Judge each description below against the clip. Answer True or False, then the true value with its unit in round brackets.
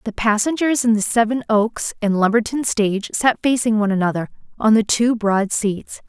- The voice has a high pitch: True (220 Hz)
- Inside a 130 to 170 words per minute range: False (180 wpm)